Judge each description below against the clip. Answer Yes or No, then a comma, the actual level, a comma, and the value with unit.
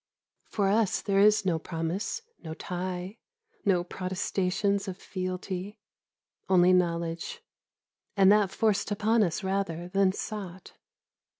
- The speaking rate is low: Yes, slow, 115 wpm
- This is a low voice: No, high, 190 Hz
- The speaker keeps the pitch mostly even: Yes, narrow, 2.1 semitones